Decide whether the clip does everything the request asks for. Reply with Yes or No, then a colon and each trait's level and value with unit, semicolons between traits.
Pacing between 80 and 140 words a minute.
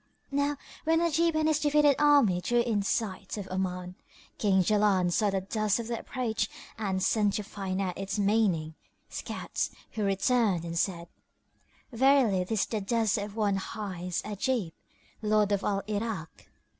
No: average, 160 wpm